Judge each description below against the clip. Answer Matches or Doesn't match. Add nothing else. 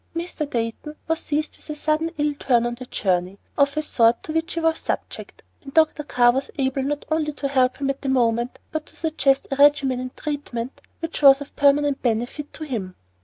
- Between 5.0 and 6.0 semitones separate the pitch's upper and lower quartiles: Doesn't match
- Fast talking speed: Matches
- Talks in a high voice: Matches